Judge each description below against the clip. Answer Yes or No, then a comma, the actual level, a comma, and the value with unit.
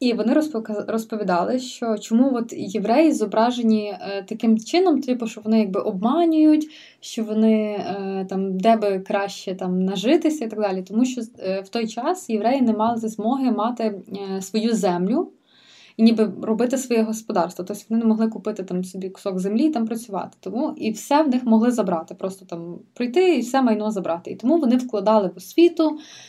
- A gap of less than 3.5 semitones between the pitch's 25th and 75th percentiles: No, average, 3.8 semitones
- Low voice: No, high, 220 Hz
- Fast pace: Yes, fast, 170 wpm